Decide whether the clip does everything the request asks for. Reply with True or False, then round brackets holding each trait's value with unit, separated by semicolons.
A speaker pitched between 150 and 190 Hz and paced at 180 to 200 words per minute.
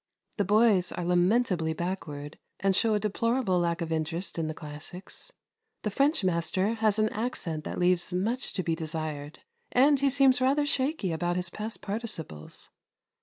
False (185 Hz; 165 wpm)